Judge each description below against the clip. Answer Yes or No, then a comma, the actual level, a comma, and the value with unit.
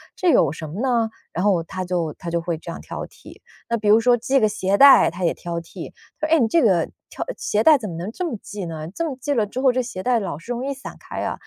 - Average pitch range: No, wide, 6.6 semitones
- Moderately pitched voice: No, high, 210 Hz